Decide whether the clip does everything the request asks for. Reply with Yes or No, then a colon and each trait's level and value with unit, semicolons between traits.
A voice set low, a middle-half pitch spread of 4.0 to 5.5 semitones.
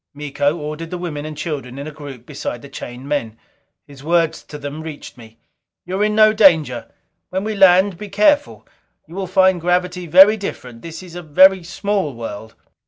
No: medium, 165 Hz; average, 4.8 semitones